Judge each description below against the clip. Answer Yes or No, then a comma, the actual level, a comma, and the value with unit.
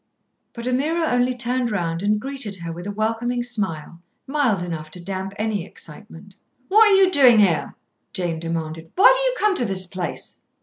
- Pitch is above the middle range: Yes, high, 210 Hz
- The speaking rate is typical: Yes, average, 180 wpm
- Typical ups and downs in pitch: No, wide, 6.4 semitones